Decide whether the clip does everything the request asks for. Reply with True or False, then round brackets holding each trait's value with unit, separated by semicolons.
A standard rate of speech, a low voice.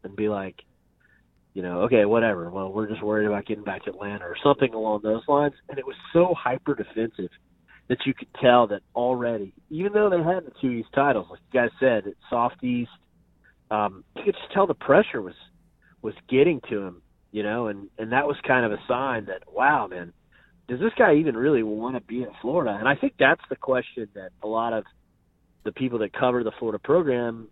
False (220 wpm; 120 Hz)